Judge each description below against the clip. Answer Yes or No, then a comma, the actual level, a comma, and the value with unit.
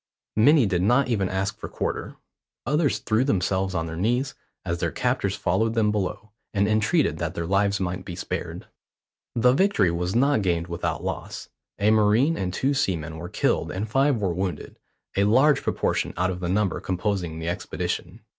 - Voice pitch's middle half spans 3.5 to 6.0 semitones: Yes, average, 4.7 semitones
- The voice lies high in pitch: No, low, 100 Hz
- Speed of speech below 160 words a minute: No, average, 180 wpm